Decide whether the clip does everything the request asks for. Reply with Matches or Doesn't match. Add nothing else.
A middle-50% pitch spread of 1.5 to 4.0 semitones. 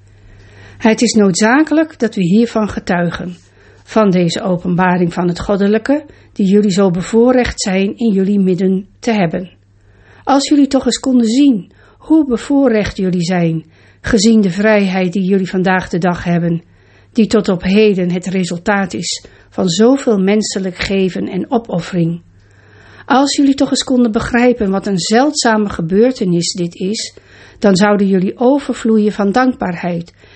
Doesn't match